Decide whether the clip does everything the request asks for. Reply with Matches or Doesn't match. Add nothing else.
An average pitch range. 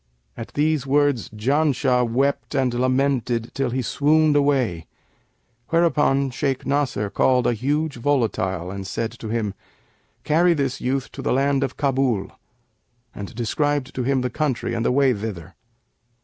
Matches